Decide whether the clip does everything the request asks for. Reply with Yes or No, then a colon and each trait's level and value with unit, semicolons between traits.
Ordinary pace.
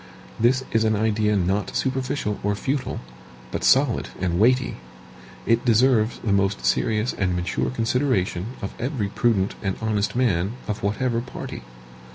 Yes: average, 145 wpm